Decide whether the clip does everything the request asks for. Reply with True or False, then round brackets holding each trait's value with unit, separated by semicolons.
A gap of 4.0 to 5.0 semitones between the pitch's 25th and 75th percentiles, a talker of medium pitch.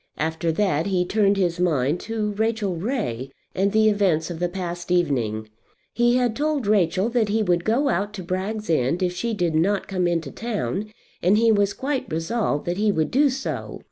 False (4.3 semitones; 195 Hz)